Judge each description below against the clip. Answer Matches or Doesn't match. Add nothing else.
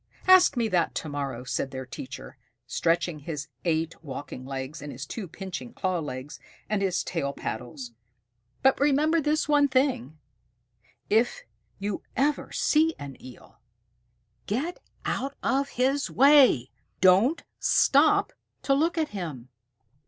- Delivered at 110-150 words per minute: Matches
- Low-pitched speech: Doesn't match